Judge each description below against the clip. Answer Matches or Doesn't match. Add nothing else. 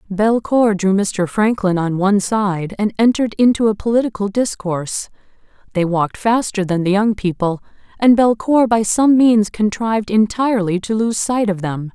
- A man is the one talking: Doesn't match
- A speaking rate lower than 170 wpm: Matches